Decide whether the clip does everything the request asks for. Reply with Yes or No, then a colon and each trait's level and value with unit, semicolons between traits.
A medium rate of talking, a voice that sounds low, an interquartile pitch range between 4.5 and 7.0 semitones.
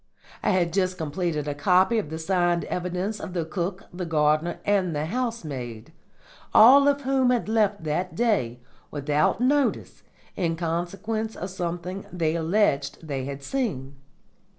No: average, 150 wpm; medium, 180 Hz; average, 4.9 semitones